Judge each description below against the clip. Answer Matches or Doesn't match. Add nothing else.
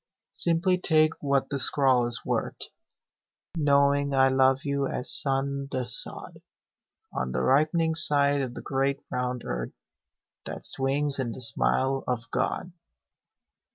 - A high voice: Doesn't match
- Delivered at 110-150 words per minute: Matches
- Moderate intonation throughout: Doesn't match